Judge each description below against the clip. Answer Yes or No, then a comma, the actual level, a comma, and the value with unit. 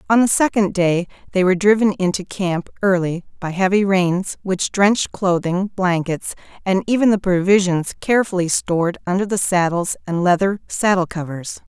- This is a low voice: No, medium, 185 Hz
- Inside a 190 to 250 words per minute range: No, average, 155 wpm